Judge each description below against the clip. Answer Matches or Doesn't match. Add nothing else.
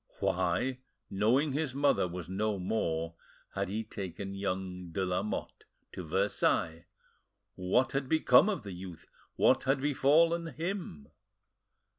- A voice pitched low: Matches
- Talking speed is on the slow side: Matches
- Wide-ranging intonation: Matches